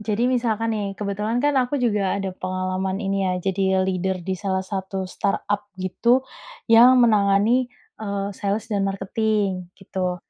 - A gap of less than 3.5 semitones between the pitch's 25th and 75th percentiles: Yes, average, 2.7 semitones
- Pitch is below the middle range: No, high, 200 Hz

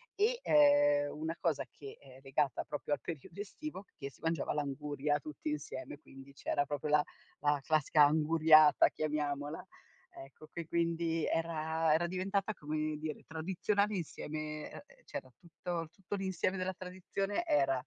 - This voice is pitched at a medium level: Yes, medium, 155 Hz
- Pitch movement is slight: No, average, 3.7 semitones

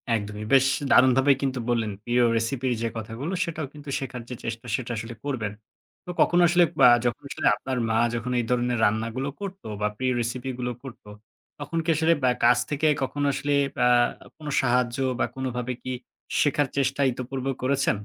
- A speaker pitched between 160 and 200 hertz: No, low, 130 Hz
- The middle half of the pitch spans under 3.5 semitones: Yes, average, 2.9 semitones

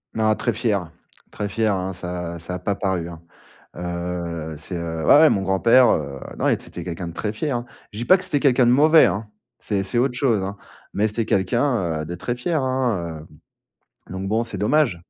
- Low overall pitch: Yes, low, 100 Hz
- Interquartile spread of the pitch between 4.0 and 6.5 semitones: Yes, wide, 5.4 semitones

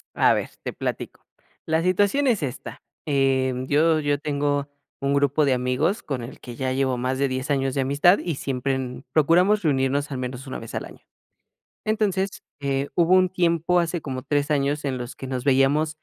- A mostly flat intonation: No, average, 3.6 semitones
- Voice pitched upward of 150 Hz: No, medium, 140 Hz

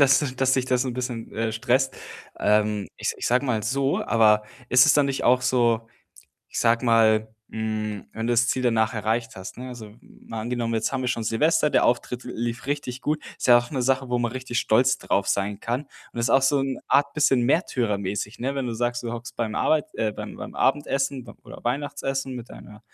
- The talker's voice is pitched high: No, low, 120 Hz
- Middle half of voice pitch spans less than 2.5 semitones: No, average, 2.9 semitones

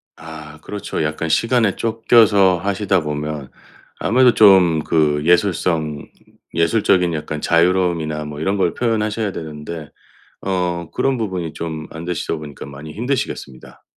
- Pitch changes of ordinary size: Yes, average, 4.6 semitones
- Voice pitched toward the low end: Yes, very low, 85 Hz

